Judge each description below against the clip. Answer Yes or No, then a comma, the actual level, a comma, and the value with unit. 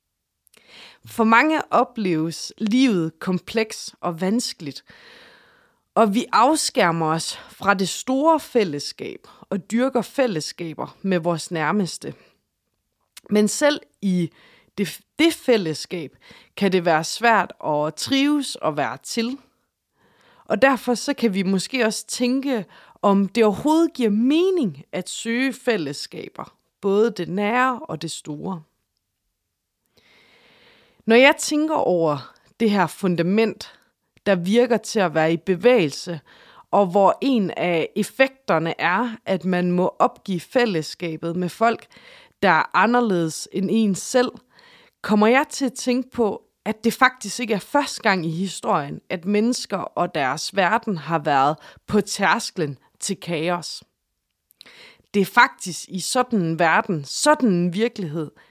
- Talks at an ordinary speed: No, slow, 130 wpm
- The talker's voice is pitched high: Yes, high, 200 Hz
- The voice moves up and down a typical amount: No, wide, 5.9 semitones